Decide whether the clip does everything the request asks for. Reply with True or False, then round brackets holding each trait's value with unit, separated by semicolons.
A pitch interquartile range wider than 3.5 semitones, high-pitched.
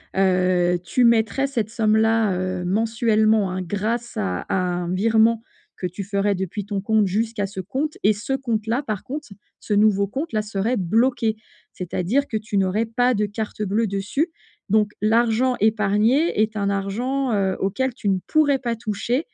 False (3.0 semitones; 215 Hz)